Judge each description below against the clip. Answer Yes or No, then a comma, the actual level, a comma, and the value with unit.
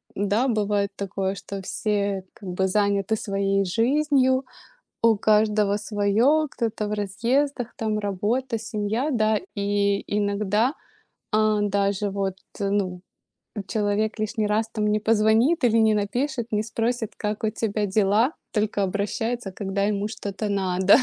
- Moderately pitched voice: No, high, 210 Hz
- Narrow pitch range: Yes, narrow, 2.0 semitones